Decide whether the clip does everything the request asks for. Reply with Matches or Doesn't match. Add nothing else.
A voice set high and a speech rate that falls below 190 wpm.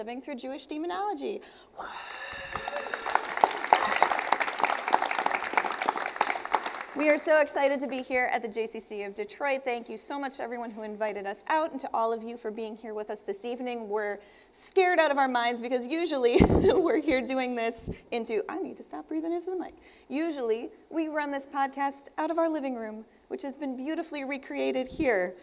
Matches